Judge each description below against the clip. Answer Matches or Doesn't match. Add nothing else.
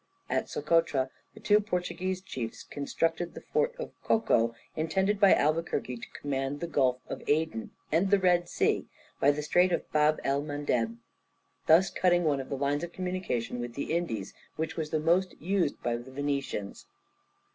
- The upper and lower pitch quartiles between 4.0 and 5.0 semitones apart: Matches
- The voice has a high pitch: Doesn't match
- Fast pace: Doesn't match